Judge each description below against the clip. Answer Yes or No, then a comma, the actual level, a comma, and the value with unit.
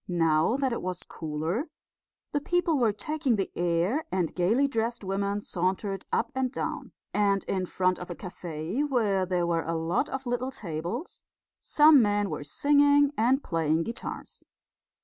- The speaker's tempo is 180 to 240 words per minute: No, average, 160 wpm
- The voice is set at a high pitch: Yes, high, 200 Hz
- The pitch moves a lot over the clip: Yes, wide, 7.1 semitones